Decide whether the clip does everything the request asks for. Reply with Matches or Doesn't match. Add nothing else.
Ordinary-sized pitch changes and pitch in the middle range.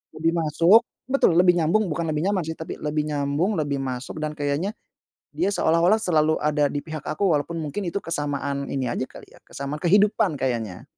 Matches